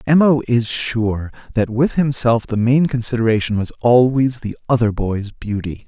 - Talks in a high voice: No, low, 120 Hz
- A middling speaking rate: Yes, average, 165 wpm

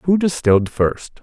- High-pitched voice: No, medium, 140 Hz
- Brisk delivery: No, average, 145 wpm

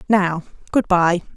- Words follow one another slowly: Yes, slow, 130 wpm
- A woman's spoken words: Yes, female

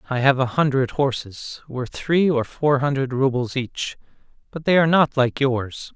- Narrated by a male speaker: Yes, male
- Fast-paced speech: No, average, 180 wpm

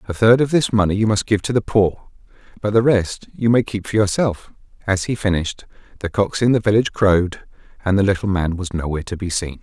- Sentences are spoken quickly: Yes, fast, 230 wpm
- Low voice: Yes, low, 100 Hz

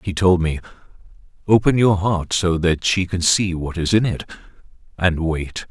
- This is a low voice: Yes, very low, 90 Hz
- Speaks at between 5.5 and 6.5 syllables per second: No, 4.5 syllables/s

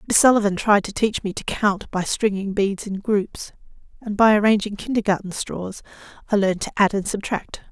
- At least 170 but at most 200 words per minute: Yes, average, 185 wpm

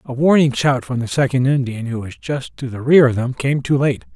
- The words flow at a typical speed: No, fast, 260 wpm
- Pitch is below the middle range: Yes, low, 130 Hz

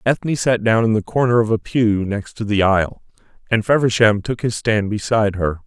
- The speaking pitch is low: Yes, low, 110 Hz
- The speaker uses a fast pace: Yes, fast, 210 wpm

